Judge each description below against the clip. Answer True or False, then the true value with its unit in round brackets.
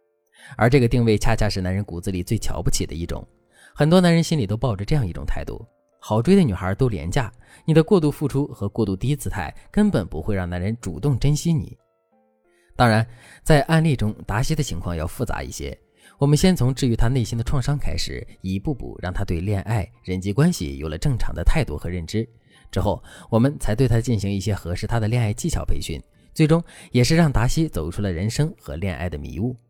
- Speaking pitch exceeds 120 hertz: False (115 Hz)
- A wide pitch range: True (7.1 semitones)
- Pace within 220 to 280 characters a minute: False (320 characters per minute)